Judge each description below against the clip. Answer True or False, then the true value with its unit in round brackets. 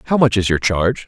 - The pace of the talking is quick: True (280 wpm)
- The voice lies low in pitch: True (105 Hz)